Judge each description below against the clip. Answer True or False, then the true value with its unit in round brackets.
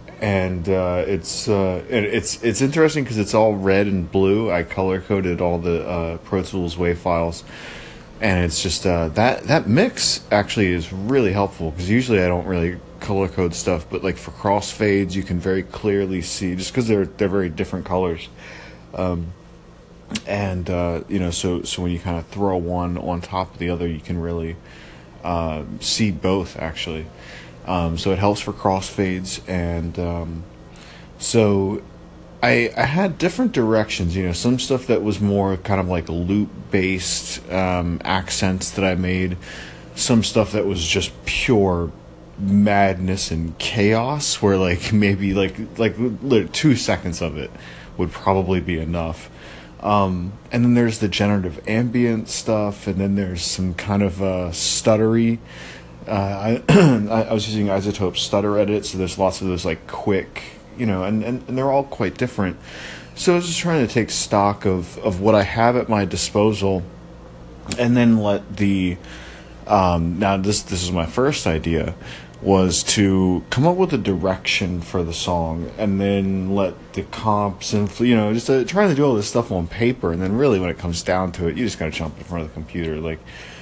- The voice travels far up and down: False (3.3 semitones)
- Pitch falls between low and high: False (95 Hz)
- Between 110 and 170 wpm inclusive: False (180 wpm)